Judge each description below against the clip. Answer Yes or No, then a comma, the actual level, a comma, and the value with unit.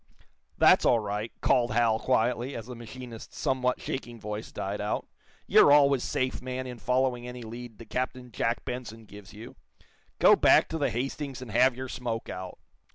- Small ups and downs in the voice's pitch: Yes, narrow, 2.3 semitones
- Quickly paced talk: No, average, 175 wpm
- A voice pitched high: No, low, 120 Hz